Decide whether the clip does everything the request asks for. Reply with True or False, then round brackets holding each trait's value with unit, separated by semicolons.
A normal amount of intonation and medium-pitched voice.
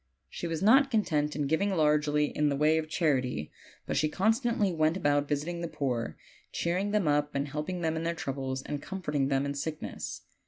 True (3.2 semitones; 155 Hz)